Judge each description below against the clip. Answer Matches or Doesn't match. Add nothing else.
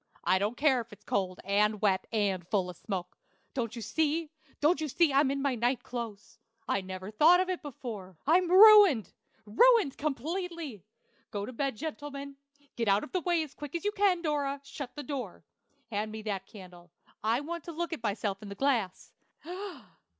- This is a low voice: Doesn't match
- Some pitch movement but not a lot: Doesn't match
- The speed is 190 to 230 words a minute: Matches